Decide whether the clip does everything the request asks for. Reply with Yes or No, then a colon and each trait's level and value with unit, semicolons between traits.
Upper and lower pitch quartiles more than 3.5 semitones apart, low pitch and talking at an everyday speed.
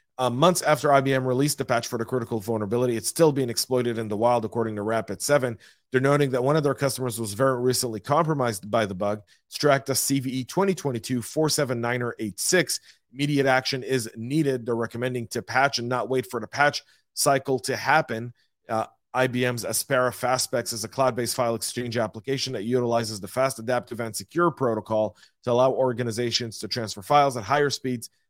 No: average, 2.7 semitones; low, 125 Hz; average, 170 wpm